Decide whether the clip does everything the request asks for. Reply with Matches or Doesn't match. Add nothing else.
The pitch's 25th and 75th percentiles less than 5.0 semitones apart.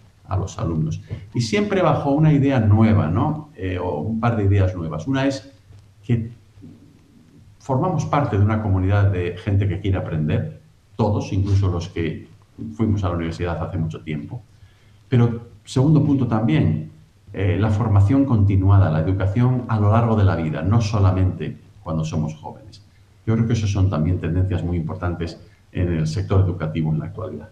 Matches